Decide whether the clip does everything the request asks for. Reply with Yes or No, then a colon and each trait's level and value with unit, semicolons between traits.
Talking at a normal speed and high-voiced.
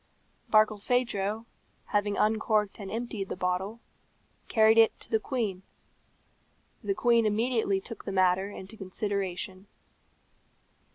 No: slow, 110 wpm; high, 210 Hz